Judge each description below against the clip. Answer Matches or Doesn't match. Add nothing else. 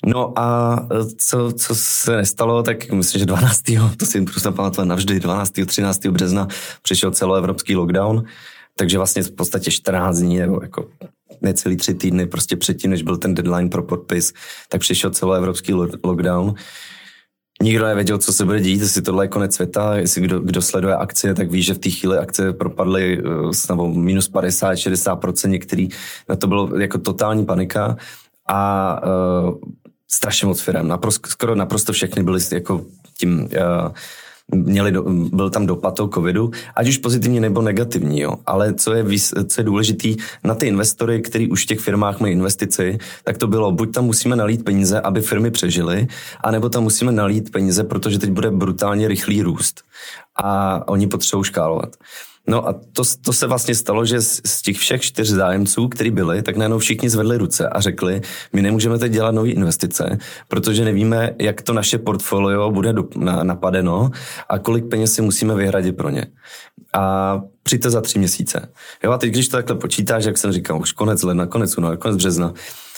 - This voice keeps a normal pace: Doesn't match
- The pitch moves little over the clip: Doesn't match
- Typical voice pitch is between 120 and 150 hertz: Doesn't match